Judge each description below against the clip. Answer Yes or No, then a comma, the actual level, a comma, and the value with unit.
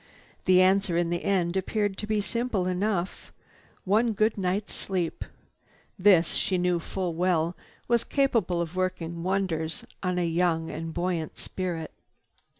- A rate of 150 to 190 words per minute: No, slow, 135 wpm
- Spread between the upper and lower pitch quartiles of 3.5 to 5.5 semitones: No, narrow, 2.4 semitones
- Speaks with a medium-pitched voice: Yes, medium, 180 Hz